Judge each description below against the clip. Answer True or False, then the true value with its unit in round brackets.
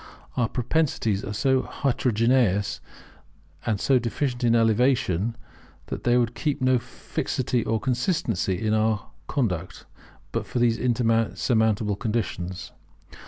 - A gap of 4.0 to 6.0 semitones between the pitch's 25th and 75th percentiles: False (3.0 semitones)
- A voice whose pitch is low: True (115 Hz)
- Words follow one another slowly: True (115 wpm)